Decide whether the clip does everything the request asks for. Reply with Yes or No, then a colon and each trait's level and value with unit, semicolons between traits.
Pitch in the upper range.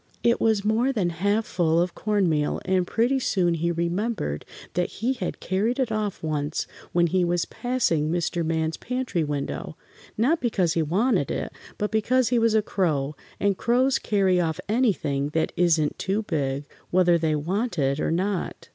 No: medium, 180 Hz